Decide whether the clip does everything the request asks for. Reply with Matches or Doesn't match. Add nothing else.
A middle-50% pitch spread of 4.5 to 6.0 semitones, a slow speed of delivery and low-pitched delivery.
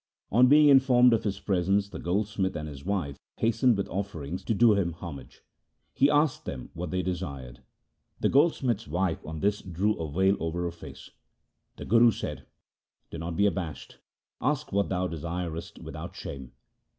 Doesn't match